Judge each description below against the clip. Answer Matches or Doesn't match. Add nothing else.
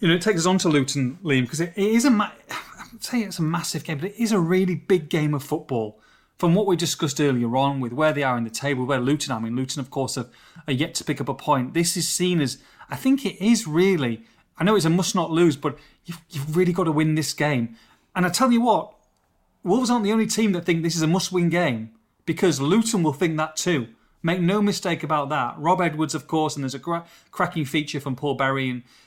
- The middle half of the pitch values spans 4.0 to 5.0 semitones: Matches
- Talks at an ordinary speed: Doesn't match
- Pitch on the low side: Doesn't match